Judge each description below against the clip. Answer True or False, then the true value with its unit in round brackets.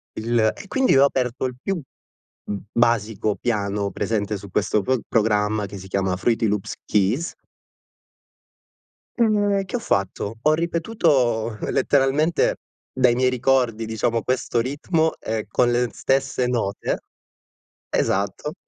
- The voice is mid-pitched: False (120 Hz)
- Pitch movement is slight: False (4.5 semitones)